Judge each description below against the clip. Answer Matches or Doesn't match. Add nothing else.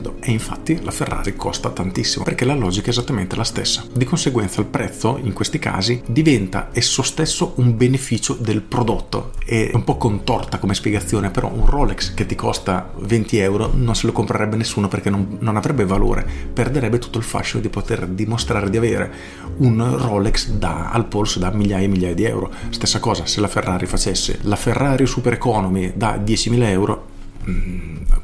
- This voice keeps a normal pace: Doesn't match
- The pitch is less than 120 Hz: Matches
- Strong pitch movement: Doesn't match